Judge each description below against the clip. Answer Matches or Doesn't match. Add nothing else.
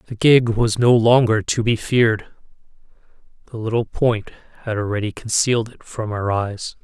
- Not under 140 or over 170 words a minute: Matches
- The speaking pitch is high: Doesn't match